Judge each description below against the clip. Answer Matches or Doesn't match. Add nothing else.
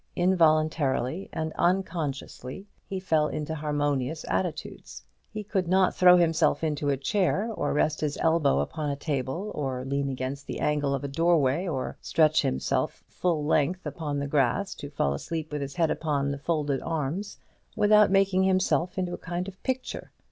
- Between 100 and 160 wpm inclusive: Doesn't match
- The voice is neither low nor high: Matches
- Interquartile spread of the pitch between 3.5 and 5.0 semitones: Matches